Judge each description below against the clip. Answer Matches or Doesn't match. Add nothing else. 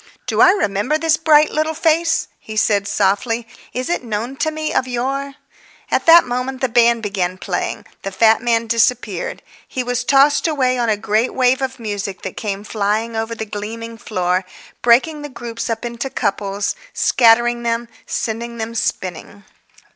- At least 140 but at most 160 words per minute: Doesn't match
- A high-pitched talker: Matches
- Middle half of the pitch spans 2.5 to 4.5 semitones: Matches